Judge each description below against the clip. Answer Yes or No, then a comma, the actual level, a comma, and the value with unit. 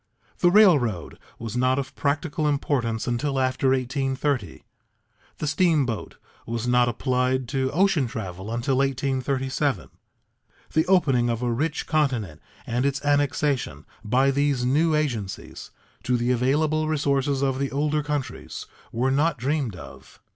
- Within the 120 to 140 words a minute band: Yes, slow, 135 wpm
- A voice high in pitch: No, low, 135 Hz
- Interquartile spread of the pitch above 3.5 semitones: No, average, 3.1 semitones